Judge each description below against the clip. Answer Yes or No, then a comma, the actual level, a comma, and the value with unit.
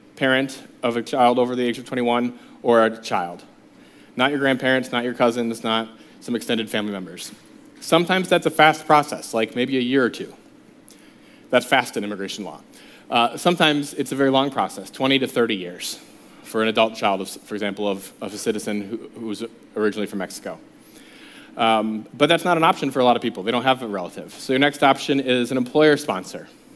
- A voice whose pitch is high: No, low, 125 Hz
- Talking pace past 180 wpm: Yes, average, 200 wpm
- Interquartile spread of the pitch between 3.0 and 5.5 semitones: Yes, average, 3.6 semitones